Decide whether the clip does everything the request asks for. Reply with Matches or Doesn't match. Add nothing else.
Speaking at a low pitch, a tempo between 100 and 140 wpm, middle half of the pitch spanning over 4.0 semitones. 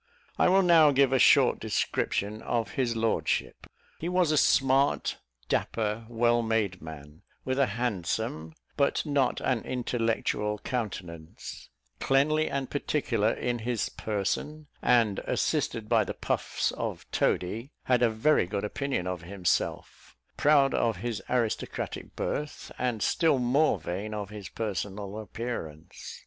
Matches